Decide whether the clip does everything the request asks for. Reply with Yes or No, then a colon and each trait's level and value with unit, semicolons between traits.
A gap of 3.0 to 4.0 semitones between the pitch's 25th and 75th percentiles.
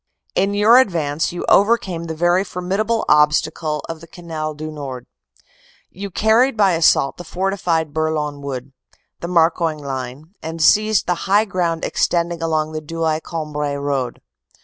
Yes: average, 3.4 semitones